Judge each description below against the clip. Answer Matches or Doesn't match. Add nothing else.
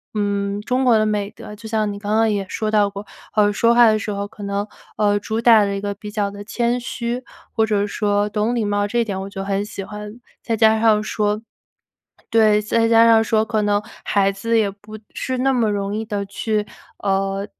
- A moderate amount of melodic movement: Doesn't match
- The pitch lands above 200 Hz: Matches